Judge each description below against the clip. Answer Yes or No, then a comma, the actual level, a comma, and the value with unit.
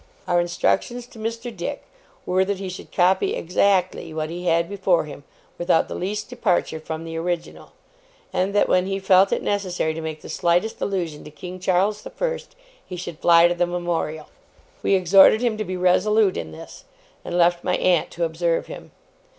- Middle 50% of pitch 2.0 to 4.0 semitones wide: Yes, narrow, 2.6 semitones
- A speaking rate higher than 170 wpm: Yes, average, 190 wpm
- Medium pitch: Yes, medium, 180 Hz